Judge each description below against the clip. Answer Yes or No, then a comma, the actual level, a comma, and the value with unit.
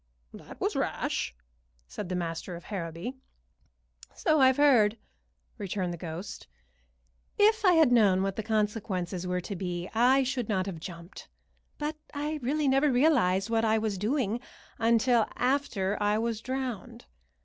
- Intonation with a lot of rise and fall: Yes, wide, 5.9 semitones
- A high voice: Yes, high, 220 Hz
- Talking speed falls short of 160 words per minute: Yes, average, 150 wpm